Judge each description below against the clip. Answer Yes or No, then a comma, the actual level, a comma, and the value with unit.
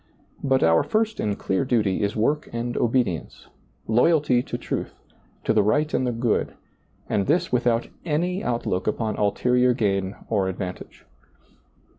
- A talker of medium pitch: No, low, 120 Hz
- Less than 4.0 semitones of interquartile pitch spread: No, average, 4.5 semitones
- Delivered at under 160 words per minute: Yes, average, 145 wpm